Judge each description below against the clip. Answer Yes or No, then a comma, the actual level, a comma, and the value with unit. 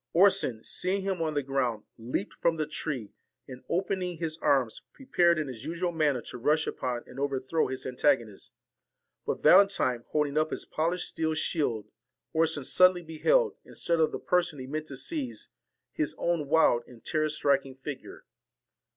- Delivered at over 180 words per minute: No, average, 170 wpm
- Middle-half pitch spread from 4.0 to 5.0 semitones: Yes, average, 4.6 semitones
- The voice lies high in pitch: No, medium, 155 Hz